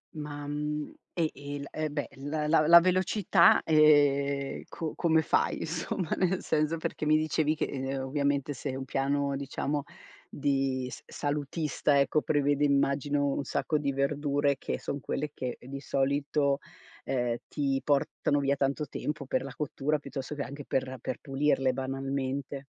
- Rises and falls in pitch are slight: Yes, narrow, 1.6 semitones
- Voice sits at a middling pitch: Yes, medium, 145 Hz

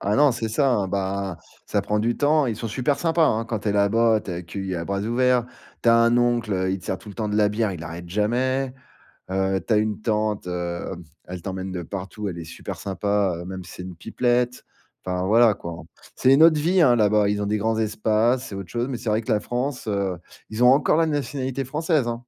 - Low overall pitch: Yes, low, 110 Hz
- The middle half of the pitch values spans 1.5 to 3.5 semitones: No, average, 4.1 semitones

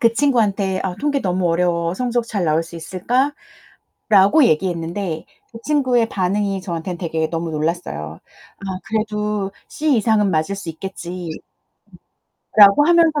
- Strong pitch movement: No, average, 5.0 semitones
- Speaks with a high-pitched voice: Yes, high, 195 Hz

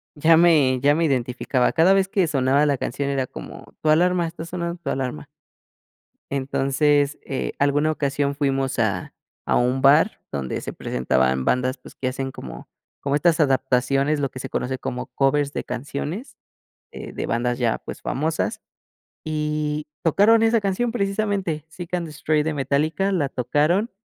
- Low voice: No, medium, 145 Hz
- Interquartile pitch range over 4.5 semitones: No, average, 3.7 semitones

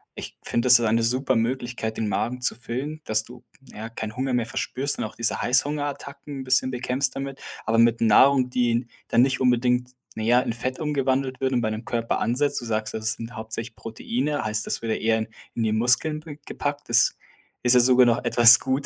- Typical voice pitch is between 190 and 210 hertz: No, low, 125 Hz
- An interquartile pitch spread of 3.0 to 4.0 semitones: No, narrow, 2.5 semitones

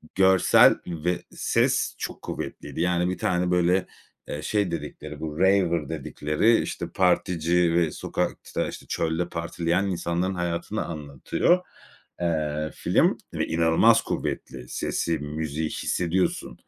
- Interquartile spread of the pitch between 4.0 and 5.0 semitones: No, narrow, 2.4 semitones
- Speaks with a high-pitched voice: No, very low, 85 Hz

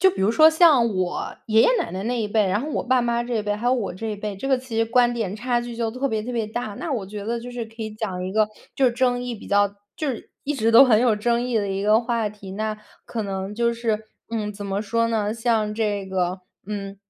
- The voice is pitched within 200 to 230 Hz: Yes, high, 225 Hz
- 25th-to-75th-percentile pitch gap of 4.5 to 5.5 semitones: No, narrow, 2.6 semitones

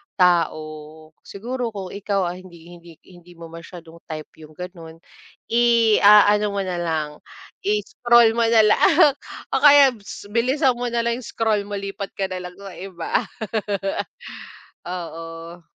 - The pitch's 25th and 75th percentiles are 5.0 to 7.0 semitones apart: Yes, wide, 5.5 semitones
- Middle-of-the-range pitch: No, high, 195 Hz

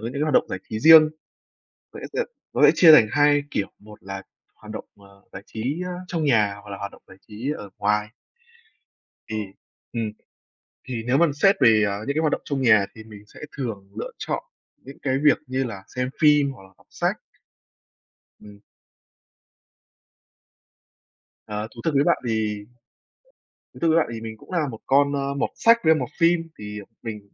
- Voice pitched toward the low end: Yes, low, 115 Hz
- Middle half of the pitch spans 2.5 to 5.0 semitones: No, wide, 5.6 semitones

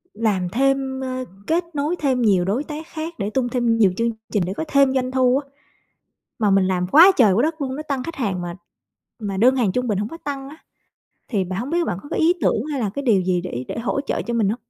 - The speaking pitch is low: No, very high, 250 Hz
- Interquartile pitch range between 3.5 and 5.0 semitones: No, wide, 5.6 semitones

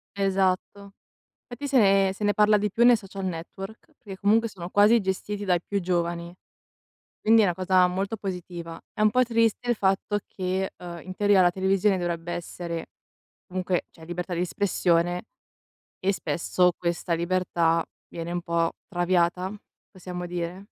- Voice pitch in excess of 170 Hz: Yes, medium, 185 Hz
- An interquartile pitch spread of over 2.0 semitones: Yes, narrow, 2.6 semitones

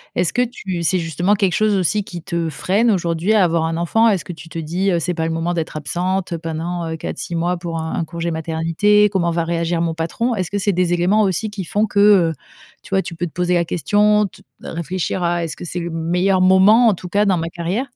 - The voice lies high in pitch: No, medium, 175 Hz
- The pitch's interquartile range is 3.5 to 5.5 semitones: No, average, 2.9 semitones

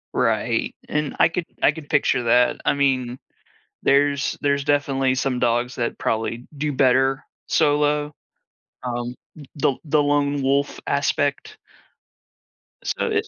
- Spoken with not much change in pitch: Yes, narrow, 2.3 semitones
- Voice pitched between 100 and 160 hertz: Yes, medium, 140 Hz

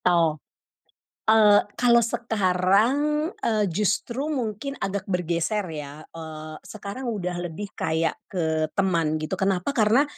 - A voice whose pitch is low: No, high, 195 Hz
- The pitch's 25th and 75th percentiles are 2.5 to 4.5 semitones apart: No, average, 5.2 semitones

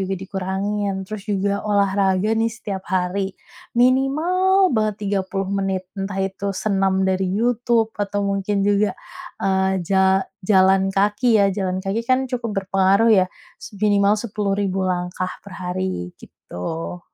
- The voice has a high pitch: Yes, high, 195 Hz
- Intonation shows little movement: Yes, narrow, 1.8 semitones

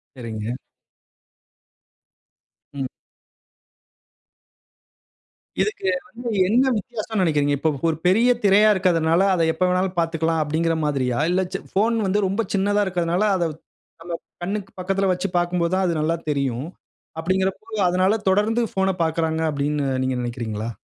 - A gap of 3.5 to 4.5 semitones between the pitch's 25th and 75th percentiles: Yes, average, 3.8 semitones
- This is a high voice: No, medium, 180 Hz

